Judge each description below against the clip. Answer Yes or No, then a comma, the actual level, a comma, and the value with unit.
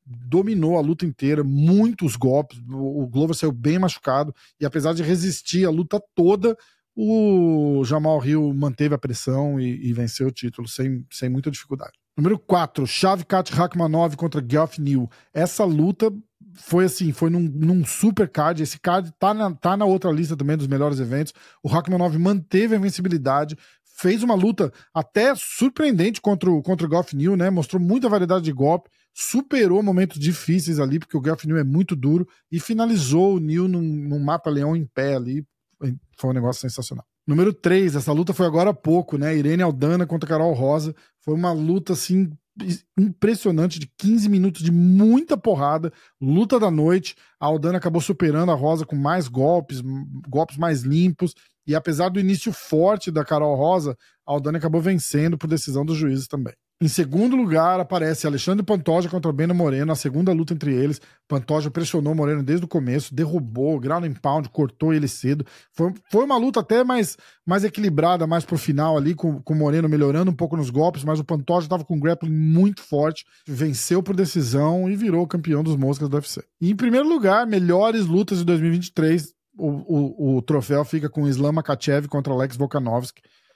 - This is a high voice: No, medium, 165 Hz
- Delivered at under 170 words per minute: No, average, 180 wpm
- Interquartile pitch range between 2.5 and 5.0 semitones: Yes, average, 3.9 semitones